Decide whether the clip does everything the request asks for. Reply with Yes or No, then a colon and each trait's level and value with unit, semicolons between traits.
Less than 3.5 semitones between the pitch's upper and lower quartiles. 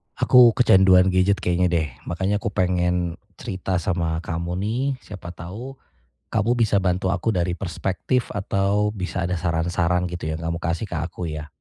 Yes: narrow, 2.6 semitones